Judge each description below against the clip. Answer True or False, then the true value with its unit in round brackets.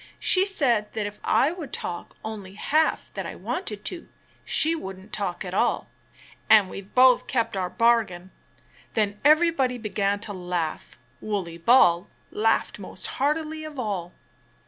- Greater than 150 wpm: False (145 wpm)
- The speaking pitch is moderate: False (215 Hz)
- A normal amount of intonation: False (6.1 semitones)